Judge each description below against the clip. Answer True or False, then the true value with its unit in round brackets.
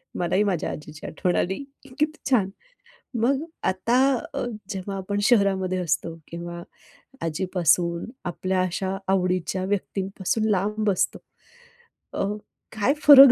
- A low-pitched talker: False (190 Hz)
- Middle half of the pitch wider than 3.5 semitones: False (2.9 semitones)